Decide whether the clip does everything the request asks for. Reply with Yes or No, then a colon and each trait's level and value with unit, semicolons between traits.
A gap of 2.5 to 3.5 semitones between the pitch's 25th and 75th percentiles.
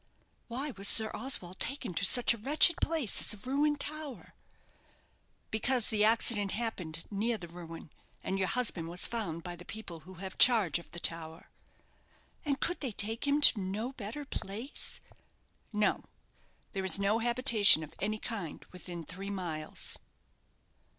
No: average, 5.3 semitones